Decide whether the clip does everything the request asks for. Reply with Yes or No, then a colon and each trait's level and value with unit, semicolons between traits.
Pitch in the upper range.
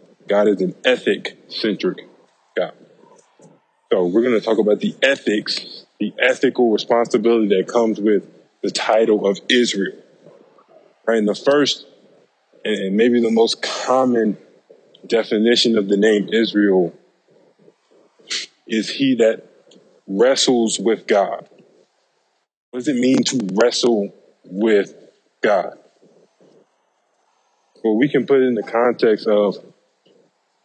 No: low, 115 Hz